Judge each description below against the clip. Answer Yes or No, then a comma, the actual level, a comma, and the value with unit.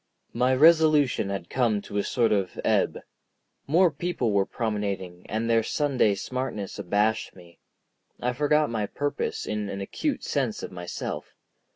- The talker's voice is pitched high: No, low, 115 Hz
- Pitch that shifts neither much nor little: No, wide, 5.8 semitones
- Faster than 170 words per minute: No, average, 150 wpm